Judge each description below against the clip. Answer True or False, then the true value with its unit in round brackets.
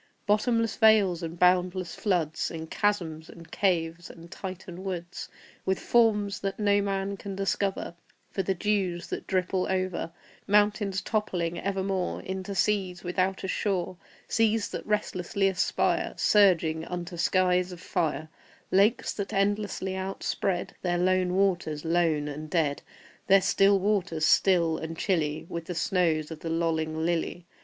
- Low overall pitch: False (185 Hz)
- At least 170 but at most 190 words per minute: False (145 wpm)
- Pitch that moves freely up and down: False (2.7 semitones)